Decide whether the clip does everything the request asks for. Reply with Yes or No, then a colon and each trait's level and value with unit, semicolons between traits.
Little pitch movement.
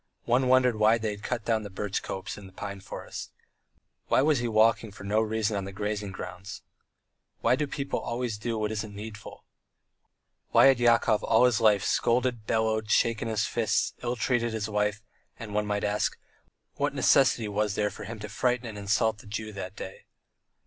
Yes: narrow, 2.2 semitones